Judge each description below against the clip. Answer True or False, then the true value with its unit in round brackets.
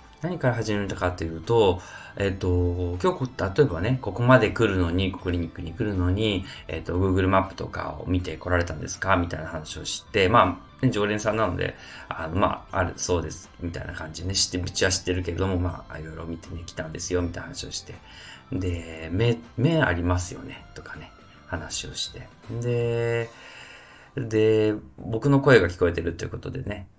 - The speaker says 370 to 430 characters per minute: True (375 characters per minute)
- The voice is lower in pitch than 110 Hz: True (95 Hz)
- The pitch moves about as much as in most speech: True (4.2 semitones)